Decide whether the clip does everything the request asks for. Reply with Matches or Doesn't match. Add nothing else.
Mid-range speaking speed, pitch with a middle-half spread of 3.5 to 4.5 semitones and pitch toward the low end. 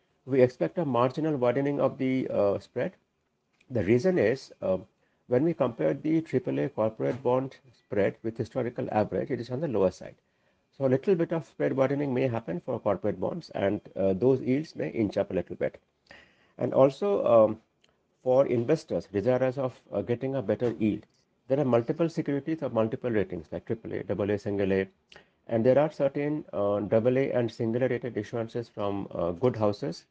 Matches